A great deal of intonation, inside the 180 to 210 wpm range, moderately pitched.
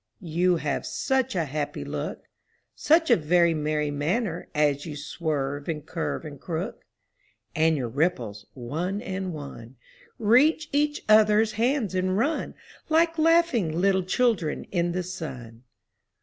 No: wide, 6.8 semitones; average, 145 wpm; medium, 175 Hz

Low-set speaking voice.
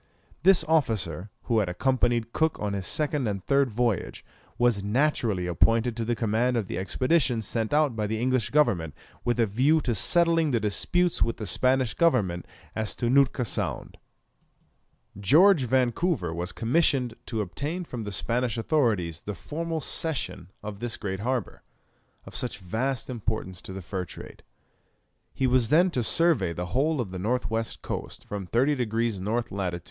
Yes: low, 115 Hz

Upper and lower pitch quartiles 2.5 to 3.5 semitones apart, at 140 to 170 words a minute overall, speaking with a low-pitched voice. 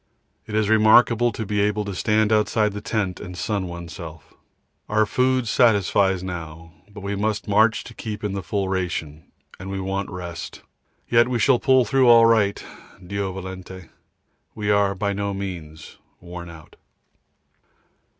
Yes: average, 2.8 semitones; average, 155 wpm; low, 100 Hz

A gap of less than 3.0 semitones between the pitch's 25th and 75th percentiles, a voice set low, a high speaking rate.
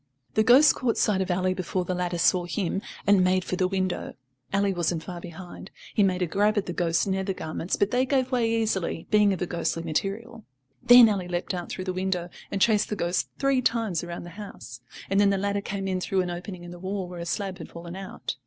No: narrow, 2.5 semitones; high, 190 Hz; fast, 235 wpm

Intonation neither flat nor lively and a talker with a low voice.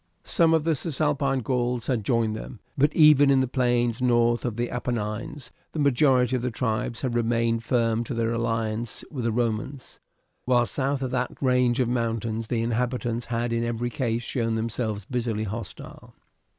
No: narrow, 2.0 semitones; low, 120 Hz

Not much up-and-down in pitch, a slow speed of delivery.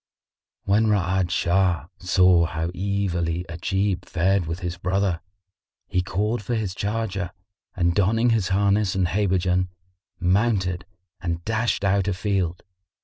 Yes: narrow, 2.3 semitones; slow, 130 wpm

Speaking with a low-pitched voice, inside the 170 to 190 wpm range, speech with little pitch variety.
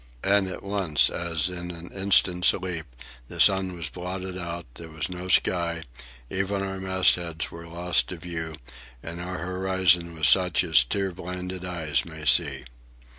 No: very low, 90 Hz; average, 160 wpm; narrow, 2.0 semitones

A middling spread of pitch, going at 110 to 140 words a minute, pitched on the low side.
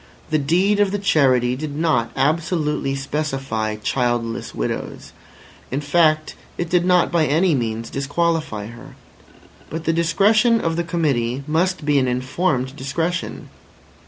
No: average, 4.6 semitones; slow, 135 wpm; medium, 150 Hz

